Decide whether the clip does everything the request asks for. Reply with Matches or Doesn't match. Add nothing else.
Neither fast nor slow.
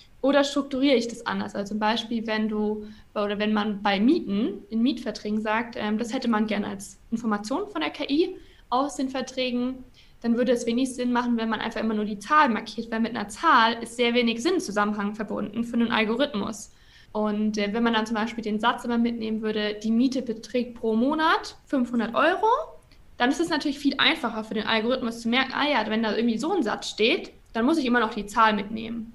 Doesn't match